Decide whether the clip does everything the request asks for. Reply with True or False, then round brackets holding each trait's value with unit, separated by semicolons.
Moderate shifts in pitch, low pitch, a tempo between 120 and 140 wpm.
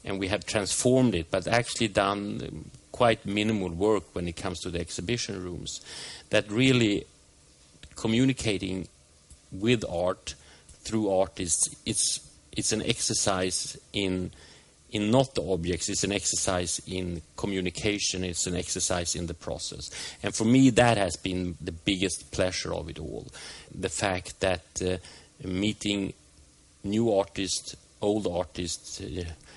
True (3.6 semitones; 95 Hz; 135 wpm)